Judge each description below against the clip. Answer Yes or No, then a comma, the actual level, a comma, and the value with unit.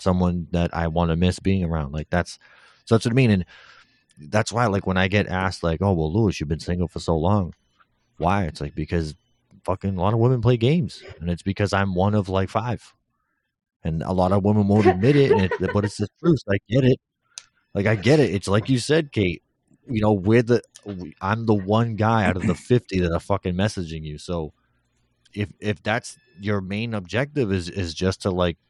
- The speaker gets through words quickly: Yes, fast, 225 wpm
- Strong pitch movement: No, average, 3.7 semitones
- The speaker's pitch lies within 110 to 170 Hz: No, low, 100 Hz